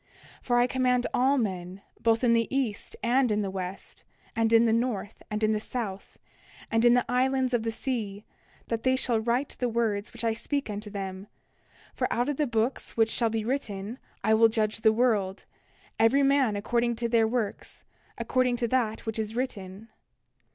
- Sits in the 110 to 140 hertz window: No, high, 230 Hz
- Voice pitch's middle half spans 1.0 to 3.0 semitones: Yes, average, 2.7 semitones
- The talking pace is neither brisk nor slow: Yes, average, 195 wpm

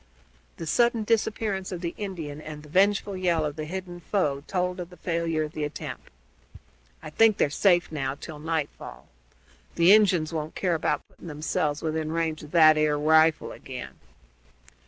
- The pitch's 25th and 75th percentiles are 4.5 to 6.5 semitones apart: No, average, 3.3 semitones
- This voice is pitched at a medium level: Yes, medium, 165 Hz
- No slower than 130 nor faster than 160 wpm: No, average, 170 wpm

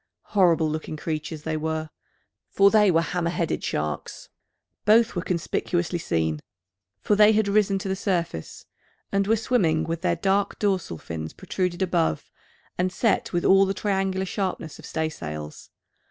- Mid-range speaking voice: Yes, medium, 175 Hz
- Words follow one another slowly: No, average, 155 wpm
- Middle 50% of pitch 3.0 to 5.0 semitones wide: Yes, average, 3.8 semitones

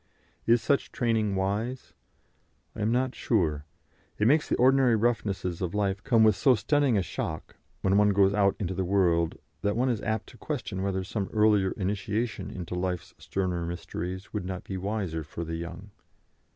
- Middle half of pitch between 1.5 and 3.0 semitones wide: No, average, 3.4 semitones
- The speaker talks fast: No, average, 180 wpm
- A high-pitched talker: No, low, 100 Hz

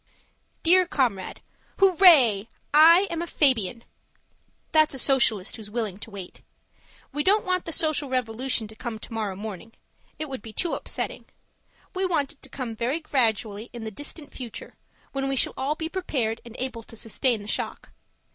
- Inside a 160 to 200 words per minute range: Yes, average, 165 wpm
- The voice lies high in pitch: Yes, very high, 255 Hz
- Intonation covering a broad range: Yes, wide, 5.8 semitones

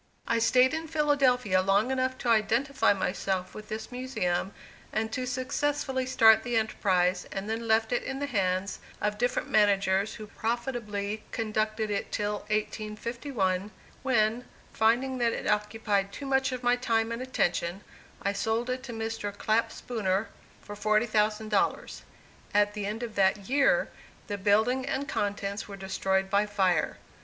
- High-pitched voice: Yes, high, 220 Hz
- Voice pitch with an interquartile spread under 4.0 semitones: Yes, average, 3.5 semitones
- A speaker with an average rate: Yes, average, 150 wpm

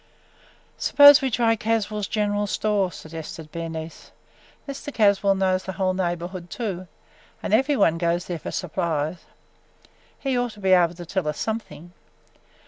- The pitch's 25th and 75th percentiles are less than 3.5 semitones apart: No, average, 4.0 semitones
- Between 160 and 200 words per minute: No, average, 145 wpm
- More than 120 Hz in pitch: Yes, high, 190 Hz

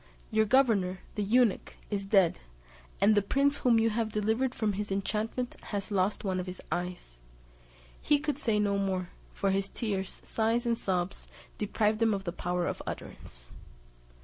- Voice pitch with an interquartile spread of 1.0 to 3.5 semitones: Yes, average, 3.0 semitones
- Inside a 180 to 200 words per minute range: No, average, 170 wpm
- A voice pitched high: Yes, high, 205 Hz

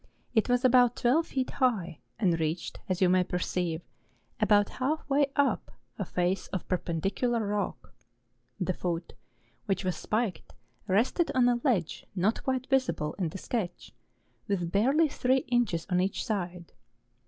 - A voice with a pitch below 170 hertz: No, high, 205 Hz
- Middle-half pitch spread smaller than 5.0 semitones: No, wide, 5.6 semitones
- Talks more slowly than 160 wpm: Yes, average, 150 wpm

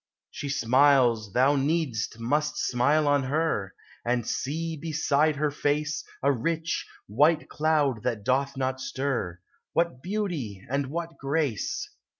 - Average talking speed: No, slow, 130 wpm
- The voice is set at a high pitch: No, medium, 140 Hz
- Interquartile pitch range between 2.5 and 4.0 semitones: Yes, average, 3.6 semitones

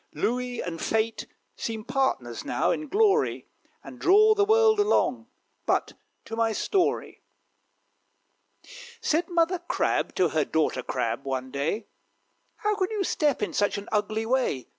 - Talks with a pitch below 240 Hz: No, very high, 250 Hz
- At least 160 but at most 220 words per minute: No, average, 140 wpm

